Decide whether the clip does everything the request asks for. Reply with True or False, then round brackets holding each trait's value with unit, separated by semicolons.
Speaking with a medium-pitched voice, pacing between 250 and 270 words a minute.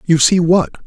False (165 Hz; 210 wpm)